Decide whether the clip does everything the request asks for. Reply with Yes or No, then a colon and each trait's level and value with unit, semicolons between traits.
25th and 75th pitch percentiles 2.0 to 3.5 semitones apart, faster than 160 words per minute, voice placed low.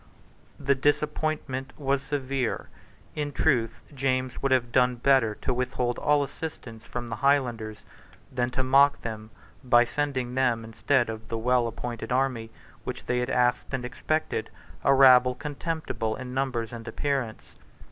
No: narrow, 2.5 semitones; average, 145 wpm; low, 125 Hz